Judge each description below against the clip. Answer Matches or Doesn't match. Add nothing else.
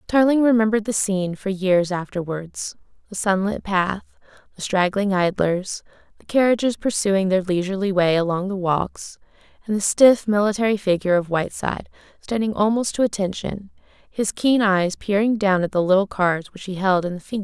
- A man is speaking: Doesn't match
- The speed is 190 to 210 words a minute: Doesn't match